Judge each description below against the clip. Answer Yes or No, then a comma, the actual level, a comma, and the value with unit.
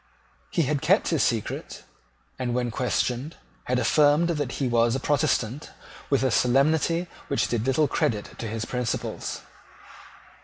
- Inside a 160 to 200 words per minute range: No, average, 145 wpm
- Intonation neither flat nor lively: Yes, average, 3.7 semitones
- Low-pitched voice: Yes, low, 130 Hz